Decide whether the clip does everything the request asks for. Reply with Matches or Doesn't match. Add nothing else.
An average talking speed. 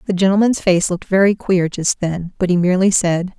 Doesn't match